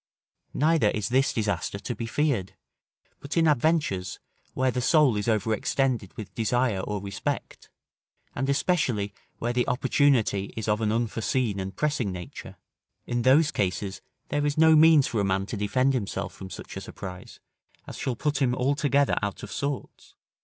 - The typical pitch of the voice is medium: No, low, 120 Hz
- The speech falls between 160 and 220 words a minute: Yes, average, 165 wpm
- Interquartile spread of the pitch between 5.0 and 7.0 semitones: Yes, wide, 5.6 semitones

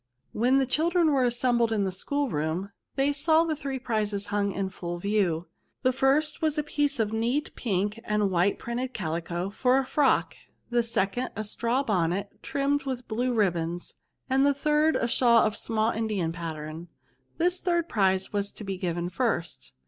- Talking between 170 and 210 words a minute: Yes, average, 185 wpm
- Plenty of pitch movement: Yes, wide, 6.0 semitones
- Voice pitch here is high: Yes, high, 225 Hz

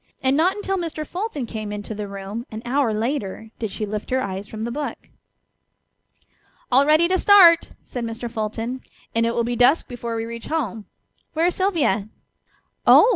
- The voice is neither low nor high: No, high, 235 Hz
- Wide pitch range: Yes, wide, 6.0 semitones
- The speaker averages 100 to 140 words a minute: No, average, 185 wpm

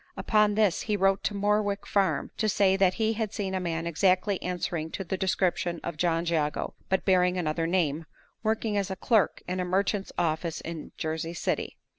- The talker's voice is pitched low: No, medium, 185 Hz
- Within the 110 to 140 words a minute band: No, average, 190 wpm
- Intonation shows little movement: No, average, 3.1 semitones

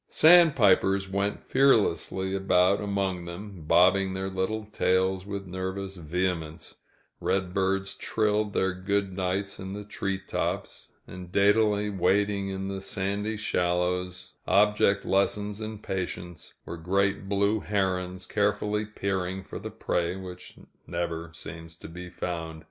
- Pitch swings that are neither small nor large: No, narrow, 1.9 semitones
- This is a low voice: Yes, very low, 95 Hz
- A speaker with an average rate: No, slow, 130 wpm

